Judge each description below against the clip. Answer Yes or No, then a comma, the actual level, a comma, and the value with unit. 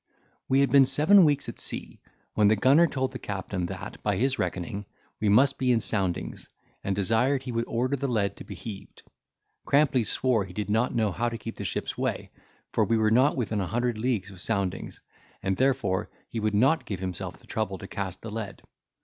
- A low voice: Yes, low, 110 Hz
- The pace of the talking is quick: Yes, fast, 210 wpm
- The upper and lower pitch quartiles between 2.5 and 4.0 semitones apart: No, average, 4.6 semitones